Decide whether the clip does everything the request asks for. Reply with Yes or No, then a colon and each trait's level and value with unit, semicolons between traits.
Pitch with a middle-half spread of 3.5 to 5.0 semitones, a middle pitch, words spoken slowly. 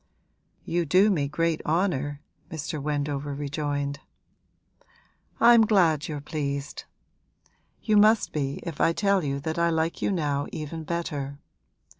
No: average, 3.1 semitones; medium, 155 Hz; slow, 130 wpm